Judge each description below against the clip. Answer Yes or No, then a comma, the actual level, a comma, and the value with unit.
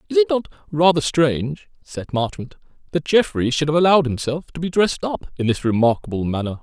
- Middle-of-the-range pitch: Yes, medium, 150 Hz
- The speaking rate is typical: Yes, average, 190 wpm